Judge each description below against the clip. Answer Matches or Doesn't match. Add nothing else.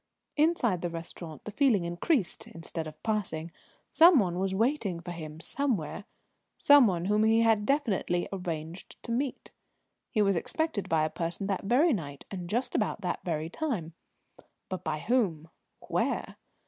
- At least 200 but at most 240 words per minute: Doesn't match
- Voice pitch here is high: Matches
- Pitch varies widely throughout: Matches